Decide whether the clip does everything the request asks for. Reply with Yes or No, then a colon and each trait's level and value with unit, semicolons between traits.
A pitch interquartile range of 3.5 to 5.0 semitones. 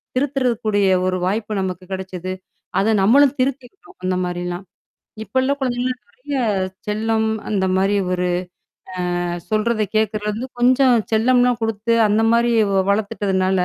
Yes: average, 4.3 semitones